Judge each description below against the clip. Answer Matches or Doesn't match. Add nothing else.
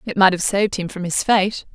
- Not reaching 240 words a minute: Doesn't match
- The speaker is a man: Doesn't match